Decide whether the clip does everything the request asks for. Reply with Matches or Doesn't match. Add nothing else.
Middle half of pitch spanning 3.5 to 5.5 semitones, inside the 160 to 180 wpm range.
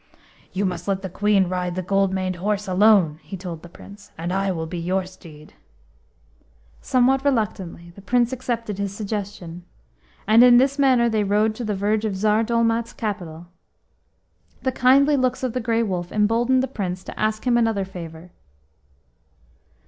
Matches